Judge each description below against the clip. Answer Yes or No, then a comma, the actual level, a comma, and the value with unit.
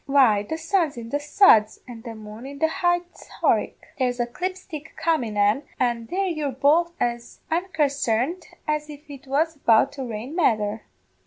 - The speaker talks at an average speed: Yes, average, 170 wpm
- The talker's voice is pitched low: No, very high, 275 Hz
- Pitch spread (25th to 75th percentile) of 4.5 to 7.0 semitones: Yes, wide, 5.5 semitones